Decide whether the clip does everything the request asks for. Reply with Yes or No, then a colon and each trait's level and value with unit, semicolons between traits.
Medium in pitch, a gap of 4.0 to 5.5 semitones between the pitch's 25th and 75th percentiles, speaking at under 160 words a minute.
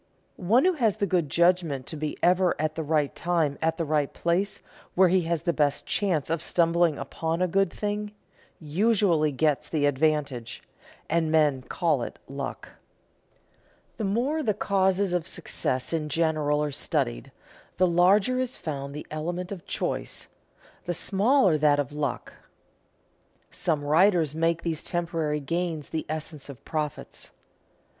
No: medium, 165 Hz; average, 3.5 semitones; average, 150 wpm